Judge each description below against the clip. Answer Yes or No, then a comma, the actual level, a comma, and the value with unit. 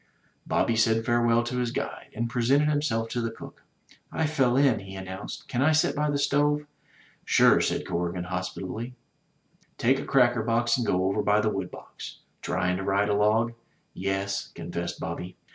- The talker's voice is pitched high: No, low, 115 Hz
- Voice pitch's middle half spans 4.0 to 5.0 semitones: Yes, average, 4.5 semitones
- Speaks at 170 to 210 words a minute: Yes, average, 180 wpm